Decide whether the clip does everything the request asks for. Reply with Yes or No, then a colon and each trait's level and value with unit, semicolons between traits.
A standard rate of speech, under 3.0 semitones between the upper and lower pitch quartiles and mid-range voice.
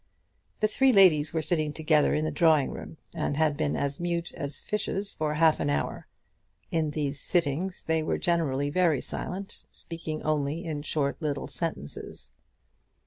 Yes: average, 160 wpm; narrow, 2.6 semitones; medium, 155 Hz